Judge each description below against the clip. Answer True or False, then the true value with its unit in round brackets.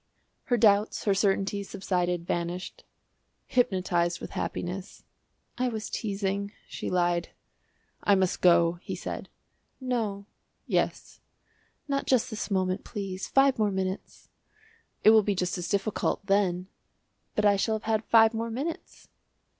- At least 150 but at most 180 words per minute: False (135 wpm)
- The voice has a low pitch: False (200 Hz)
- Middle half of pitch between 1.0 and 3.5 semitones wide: True (3.1 semitones)